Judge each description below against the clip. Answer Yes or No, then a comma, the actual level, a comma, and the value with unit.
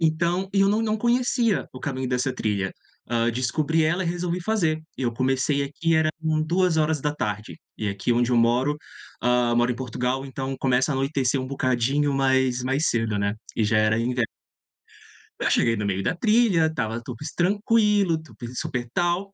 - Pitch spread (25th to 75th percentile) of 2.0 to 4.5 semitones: No, wide, 5.6 semitones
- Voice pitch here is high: No, low, 135 Hz